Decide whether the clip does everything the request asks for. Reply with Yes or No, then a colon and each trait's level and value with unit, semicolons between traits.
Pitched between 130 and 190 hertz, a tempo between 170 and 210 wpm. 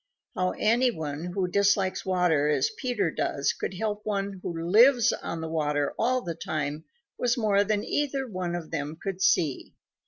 Yes: medium, 185 Hz; average, 175 wpm